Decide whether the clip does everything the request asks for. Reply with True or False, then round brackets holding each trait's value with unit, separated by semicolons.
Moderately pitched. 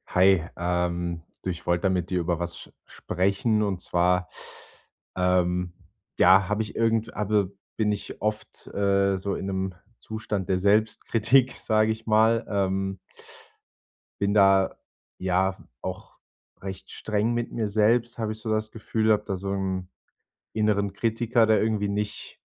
False (100 Hz)